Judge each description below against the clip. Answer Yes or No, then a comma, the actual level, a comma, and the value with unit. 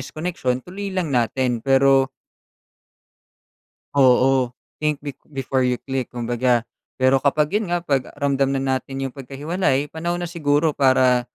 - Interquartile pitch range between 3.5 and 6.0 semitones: No, average, 2.8 semitones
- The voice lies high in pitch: No, low, 135 Hz